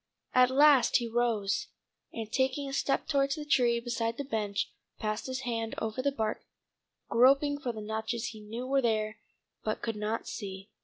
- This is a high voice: Yes, high, 235 Hz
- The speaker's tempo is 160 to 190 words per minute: Yes, average, 175 wpm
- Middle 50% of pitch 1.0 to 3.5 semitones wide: Yes, average, 3.2 semitones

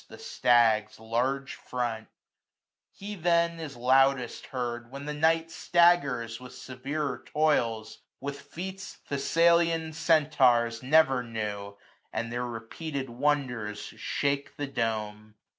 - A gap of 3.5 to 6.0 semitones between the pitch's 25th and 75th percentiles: Yes, average, 4.9 semitones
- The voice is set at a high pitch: No, low, 135 Hz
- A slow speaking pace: Yes, slow, 115 wpm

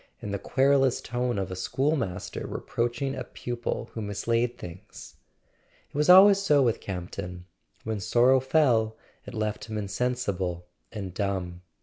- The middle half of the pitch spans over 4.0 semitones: Yes, average, 5.0 semitones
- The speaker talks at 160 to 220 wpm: No, average, 145 wpm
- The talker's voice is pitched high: No, low, 115 Hz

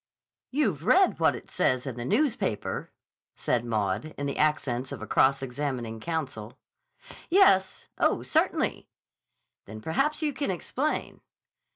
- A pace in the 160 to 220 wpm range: No, slow, 135 wpm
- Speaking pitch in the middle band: Yes, medium, 145 Hz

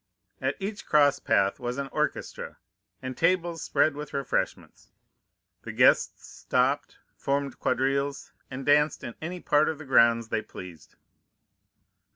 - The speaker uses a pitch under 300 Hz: Yes, medium, 140 Hz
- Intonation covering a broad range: No, average, 3.3 semitones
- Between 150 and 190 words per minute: No, slow, 135 wpm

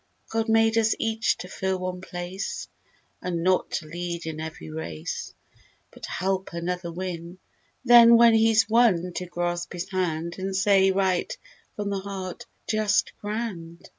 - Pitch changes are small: No, average, 3.7 semitones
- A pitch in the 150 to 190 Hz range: Yes, medium, 185 Hz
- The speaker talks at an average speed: Yes, average, 150 wpm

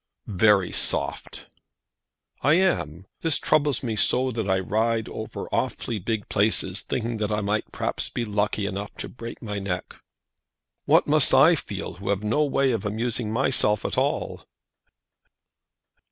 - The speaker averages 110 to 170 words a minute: Yes, average, 150 wpm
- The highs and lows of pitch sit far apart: No, average, 3.8 semitones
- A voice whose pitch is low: Yes, low, 110 Hz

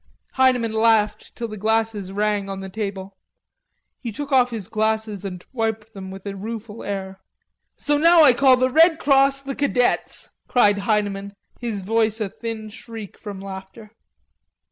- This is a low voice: No, high, 220 Hz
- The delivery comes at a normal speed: Yes, average, 160 wpm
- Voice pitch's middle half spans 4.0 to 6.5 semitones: No, average, 3.4 semitones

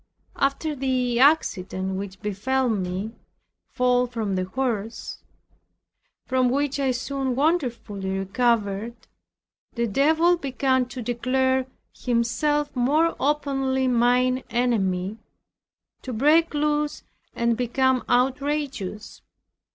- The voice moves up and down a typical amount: Yes, average, 3.2 semitones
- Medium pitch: No, very high, 250 Hz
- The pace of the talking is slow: Yes, slow, 95 wpm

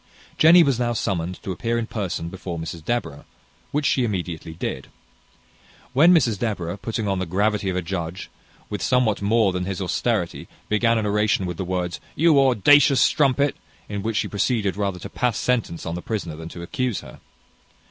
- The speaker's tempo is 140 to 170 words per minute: No, average, 185 wpm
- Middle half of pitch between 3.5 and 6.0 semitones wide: Yes, average, 4.9 semitones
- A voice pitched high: No, low, 105 Hz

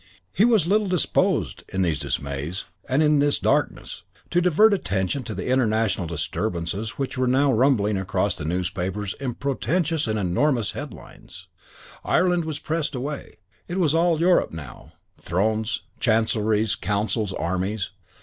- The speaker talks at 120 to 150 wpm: Yes, average, 140 wpm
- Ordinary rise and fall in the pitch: No, wide, 8.0 semitones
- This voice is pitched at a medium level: No, low, 115 Hz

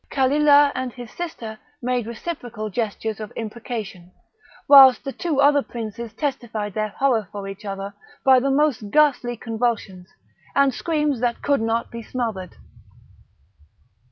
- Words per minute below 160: Yes, slow, 135 wpm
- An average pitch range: Yes, average, 4.3 semitones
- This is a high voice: Yes, high, 235 Hz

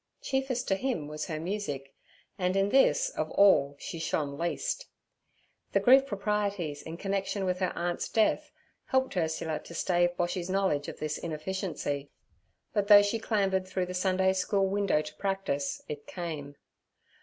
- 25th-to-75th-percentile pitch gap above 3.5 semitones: Yes, average, 4.1 semitones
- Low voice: No, medium, 185 Hz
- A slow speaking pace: No, average, 155 wpm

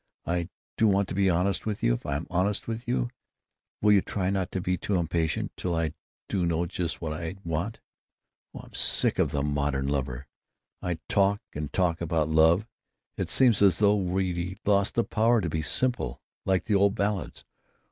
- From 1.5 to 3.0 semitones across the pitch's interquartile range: No, average, 3.8 semitones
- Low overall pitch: Yes, very low, 90 Hz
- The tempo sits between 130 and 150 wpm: No, average, 185 wpm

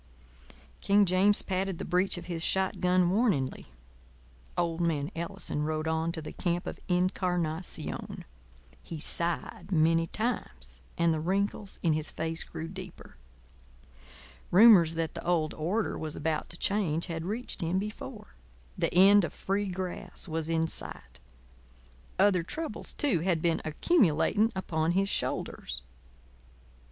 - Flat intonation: No, average, 3.0 semitones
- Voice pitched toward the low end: No, medium, 175 Hz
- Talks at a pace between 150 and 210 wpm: No, average, 140 wpm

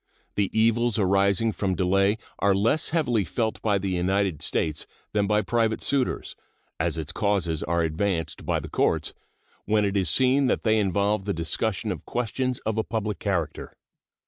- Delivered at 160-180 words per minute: Yes, average, 170 wpm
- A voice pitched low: Yes, low, 100 Hz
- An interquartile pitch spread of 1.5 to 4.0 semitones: Yes, average, 3.0 semitones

